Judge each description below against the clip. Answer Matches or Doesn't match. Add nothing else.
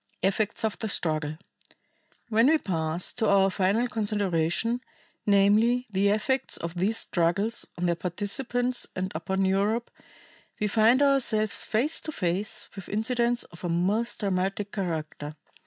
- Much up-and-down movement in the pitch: Doesn't match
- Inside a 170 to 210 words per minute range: Doesn't match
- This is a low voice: Doesn't match